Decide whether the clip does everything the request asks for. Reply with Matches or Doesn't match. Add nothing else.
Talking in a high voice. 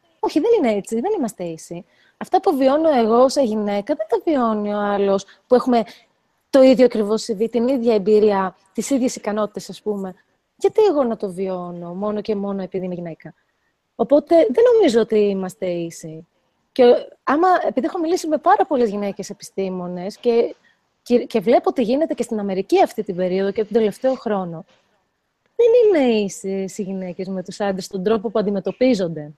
Matches